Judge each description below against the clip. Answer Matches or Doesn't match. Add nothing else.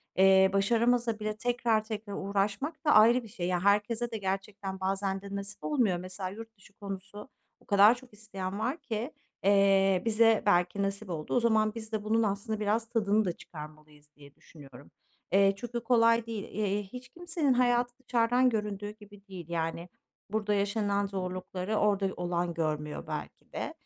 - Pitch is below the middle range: Doesn't match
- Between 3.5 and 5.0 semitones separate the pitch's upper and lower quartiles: Doesn't match